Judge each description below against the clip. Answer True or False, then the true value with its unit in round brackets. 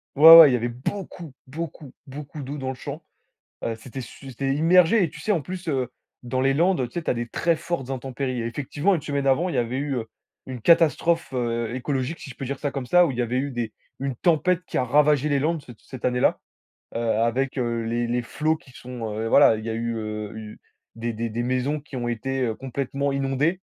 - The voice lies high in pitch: False (135 Hz)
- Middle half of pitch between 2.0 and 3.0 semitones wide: False (3.9 semitones)